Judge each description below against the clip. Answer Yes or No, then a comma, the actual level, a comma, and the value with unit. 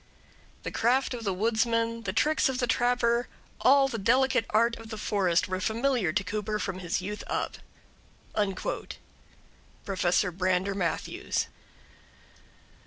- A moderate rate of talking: No, slow, 130 wpm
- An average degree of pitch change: Yes, average, 4.0 semitones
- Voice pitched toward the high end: Yes, high, 220 Hz